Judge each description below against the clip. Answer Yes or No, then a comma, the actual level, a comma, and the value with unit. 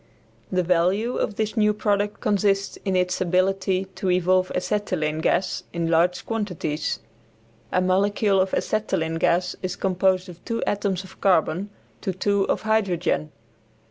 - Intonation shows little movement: Yes, narrow, 2.1 semitones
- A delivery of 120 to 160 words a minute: Yes, average, 140 wpm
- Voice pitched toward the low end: No, medium, 185 Hz